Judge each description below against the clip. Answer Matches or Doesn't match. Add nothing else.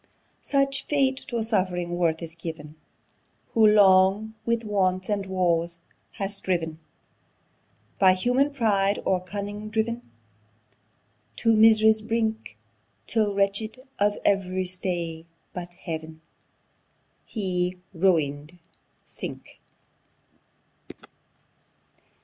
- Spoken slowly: Matches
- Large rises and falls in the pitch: Doesn't match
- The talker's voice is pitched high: Matches